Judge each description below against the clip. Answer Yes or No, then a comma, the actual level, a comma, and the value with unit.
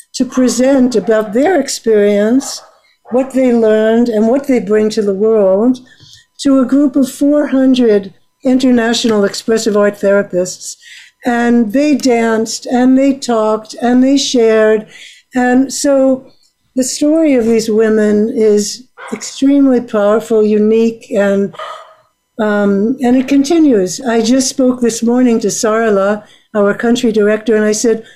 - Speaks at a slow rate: Yes, slow, 130 wpm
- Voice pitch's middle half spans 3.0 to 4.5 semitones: Yes, average, 3.3 semitones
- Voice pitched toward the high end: Yes, high, 235 Hz